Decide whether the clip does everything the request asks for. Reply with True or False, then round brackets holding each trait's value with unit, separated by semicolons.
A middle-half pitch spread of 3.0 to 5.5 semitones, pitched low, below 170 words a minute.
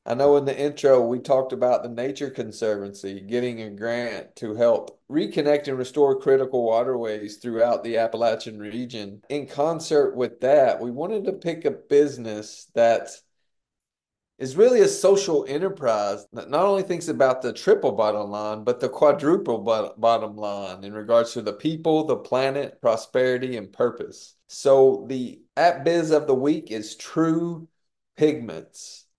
True (4.4 semitones; 125 Hz; 155 wpm)